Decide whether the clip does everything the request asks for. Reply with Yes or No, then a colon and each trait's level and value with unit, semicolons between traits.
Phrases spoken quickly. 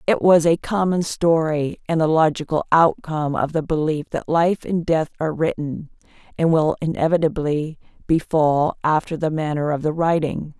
No: average, 160 wpm